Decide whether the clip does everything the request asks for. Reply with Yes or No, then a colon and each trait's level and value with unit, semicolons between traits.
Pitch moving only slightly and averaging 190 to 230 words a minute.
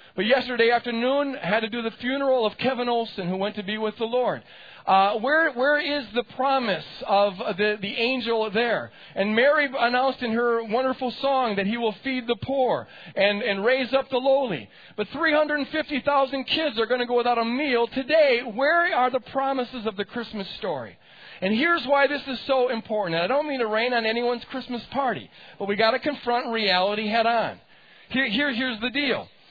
No: average, 3.3 semitones; average, 200 wpm